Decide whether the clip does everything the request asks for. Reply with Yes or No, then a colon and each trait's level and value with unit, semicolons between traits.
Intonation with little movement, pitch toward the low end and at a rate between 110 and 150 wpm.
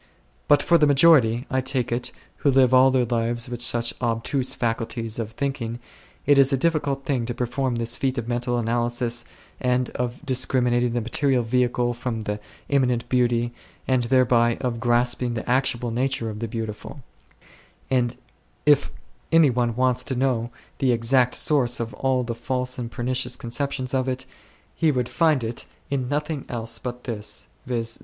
No: narrow, 1.9 semitones; low, 125 Hz; average, 170 wpm